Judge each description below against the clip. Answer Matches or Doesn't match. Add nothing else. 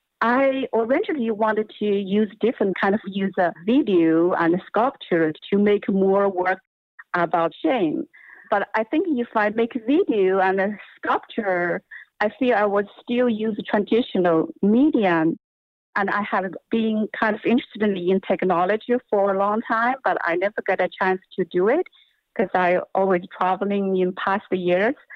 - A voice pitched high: Matches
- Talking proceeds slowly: Doesn't match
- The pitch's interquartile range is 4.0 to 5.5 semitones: Doesn't match